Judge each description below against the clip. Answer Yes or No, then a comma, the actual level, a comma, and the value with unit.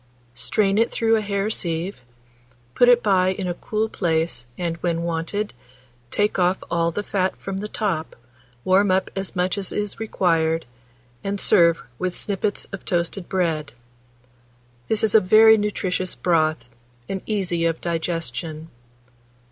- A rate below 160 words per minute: Yes, average, 150 wpm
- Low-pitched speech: No, medium, 185 Hz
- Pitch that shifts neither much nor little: Yes, average, 3.6 semitones